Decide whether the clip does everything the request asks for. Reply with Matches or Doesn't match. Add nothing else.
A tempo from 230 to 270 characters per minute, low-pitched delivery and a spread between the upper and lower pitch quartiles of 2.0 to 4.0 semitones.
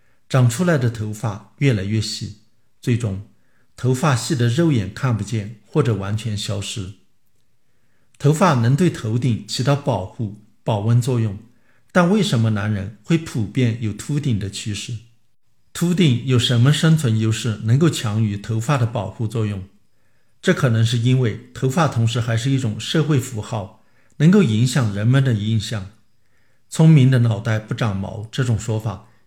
Matches